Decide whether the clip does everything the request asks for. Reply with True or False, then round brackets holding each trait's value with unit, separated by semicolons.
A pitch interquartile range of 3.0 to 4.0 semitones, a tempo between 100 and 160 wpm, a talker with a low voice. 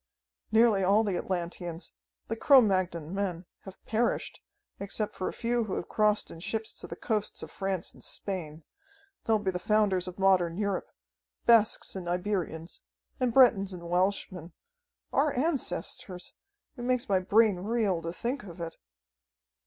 False (3.7 semitones; 155 wpm; 195 Hz)